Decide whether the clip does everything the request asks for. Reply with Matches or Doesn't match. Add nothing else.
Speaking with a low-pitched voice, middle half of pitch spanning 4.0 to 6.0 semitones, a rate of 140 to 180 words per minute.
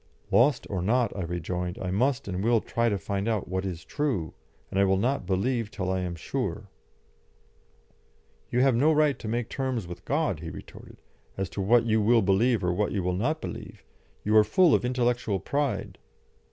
Doesn't match